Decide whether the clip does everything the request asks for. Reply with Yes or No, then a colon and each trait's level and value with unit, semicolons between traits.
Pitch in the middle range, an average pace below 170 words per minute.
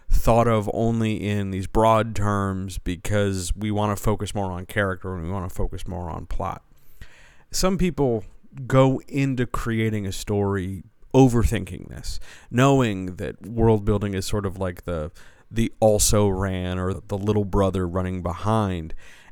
No: low, 100 Hz; average, 155 wpm